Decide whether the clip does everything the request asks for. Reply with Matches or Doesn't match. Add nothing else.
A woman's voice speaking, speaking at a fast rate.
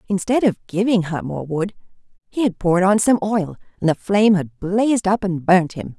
Matches